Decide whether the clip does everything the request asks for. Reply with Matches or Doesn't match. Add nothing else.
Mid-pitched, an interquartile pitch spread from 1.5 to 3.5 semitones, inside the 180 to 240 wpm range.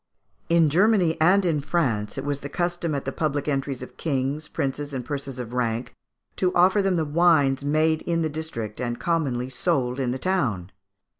Doesn't match